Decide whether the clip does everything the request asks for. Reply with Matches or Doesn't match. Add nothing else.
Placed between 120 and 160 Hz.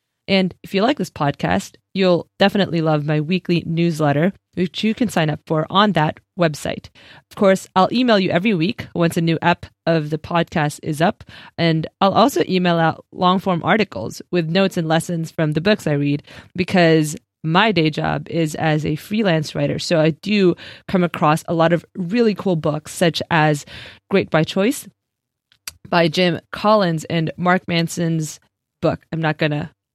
Doesn't match